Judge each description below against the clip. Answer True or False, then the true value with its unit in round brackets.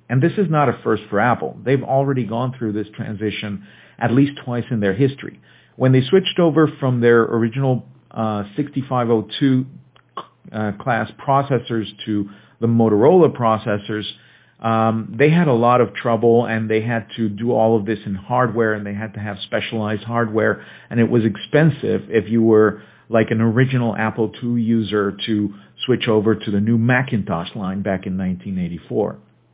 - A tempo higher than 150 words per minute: True (170 wpm)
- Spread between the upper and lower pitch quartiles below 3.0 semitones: True (2.6 semitones)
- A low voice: True (115 Hz)